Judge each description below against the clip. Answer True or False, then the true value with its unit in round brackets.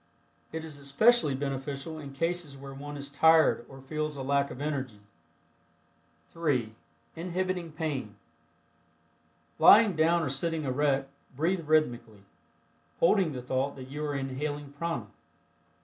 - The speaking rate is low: True (130 wpm)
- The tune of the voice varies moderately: True (3.0 semitones)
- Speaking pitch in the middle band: True (145 Hz)